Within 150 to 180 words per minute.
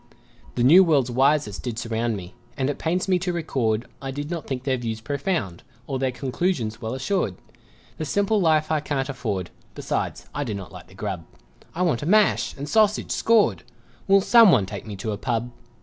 No: average, 195 wpm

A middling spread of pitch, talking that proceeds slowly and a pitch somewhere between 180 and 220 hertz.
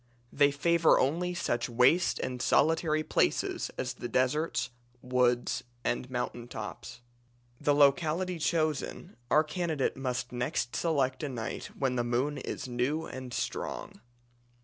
No: average, 4.0 semitones; slow, 130 wpm; low, 135 Hz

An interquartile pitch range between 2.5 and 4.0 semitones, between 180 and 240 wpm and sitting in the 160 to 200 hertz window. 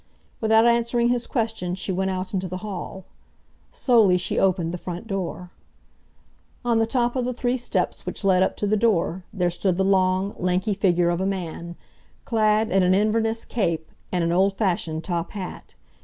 Yes: average, 3.7 semitones; average, 185 wpm; high, 190 Hz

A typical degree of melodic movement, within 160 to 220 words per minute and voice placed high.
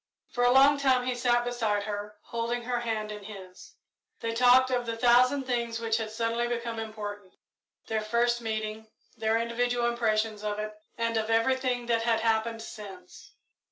No: narrow, 2.0 semitones; average, 170 wpm; high, 230 Hz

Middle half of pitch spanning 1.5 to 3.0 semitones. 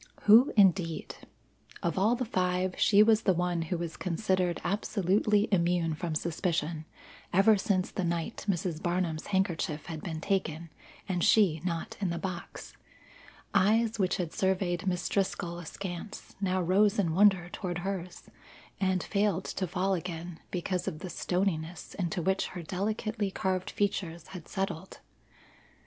Yes: narrow, 2.5 semitones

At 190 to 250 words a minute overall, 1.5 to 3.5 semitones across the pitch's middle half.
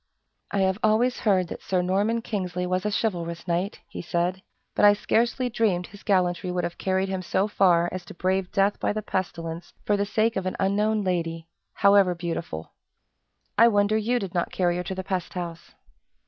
Yes: average, 195 wpm; narrow, 2.6 semitones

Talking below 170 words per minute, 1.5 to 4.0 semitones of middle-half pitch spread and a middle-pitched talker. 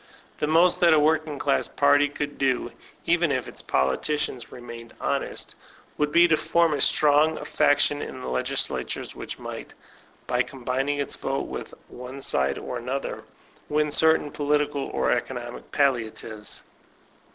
Yes: average, 150 wpm; average, 3.0 semitones; medium, 145 Hz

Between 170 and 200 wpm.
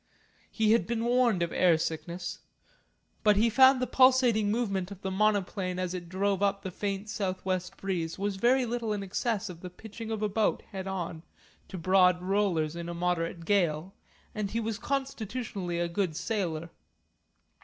Yes: average, 175 wpm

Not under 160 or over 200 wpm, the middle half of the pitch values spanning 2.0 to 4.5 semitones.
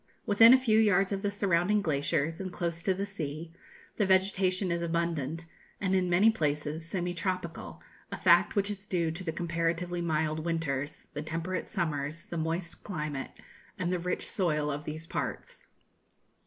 Yes: average, 170 wpm; average, 3.0 semitones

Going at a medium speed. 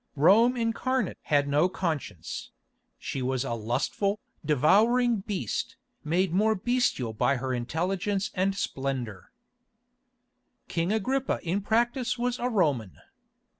No: slow, 115 wpm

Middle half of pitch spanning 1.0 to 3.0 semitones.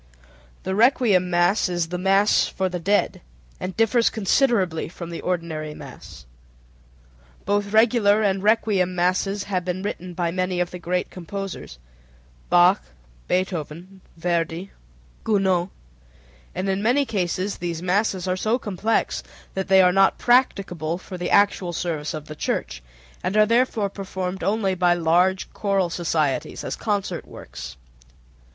Yes: narrow, 2.6 semitones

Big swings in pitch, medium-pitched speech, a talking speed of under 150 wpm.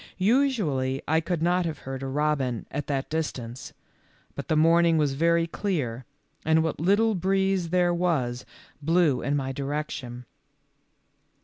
No: average, 4.6 semitones; medium, 160 Hz; average, 140 wpm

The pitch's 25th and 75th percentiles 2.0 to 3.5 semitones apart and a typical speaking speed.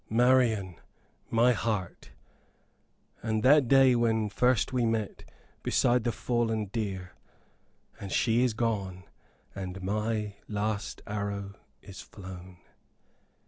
No: average, 3.1 semitones; slow, 105 wpm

